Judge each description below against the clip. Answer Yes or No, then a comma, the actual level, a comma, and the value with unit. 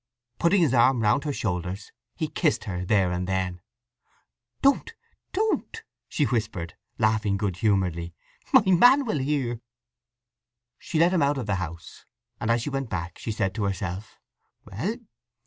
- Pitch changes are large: Yes, wide, 7.6 semitones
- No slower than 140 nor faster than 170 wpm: Yes, average, 155 wpm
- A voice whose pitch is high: No, low, 110 Hz